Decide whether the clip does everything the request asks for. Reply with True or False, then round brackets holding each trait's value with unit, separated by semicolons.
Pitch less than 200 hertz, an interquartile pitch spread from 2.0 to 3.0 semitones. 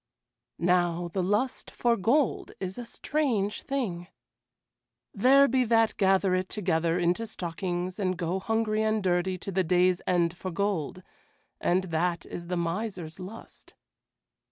False (185 Hz; 3.6 semitones)